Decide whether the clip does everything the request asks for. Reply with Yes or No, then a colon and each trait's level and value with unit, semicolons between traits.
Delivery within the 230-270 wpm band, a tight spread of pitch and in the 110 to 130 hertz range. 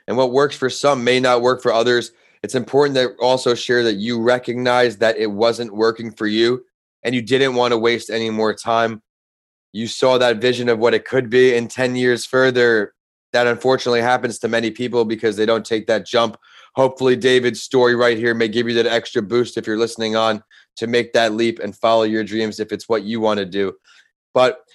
No: fast, 215 wpm; narrow, 1.8 semitones; low, 120 Hz